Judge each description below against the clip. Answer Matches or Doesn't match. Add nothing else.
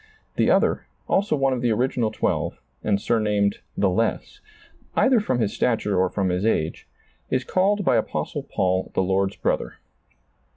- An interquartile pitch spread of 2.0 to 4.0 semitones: Doesn't match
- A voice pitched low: Matches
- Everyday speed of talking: Matches